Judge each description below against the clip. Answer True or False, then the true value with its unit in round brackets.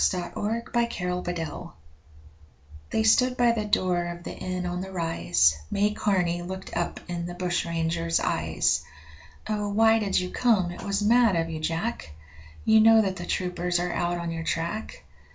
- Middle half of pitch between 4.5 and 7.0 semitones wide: False (3.6 semitones)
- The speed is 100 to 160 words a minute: False (170 wpm)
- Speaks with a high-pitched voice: False (180 Hz)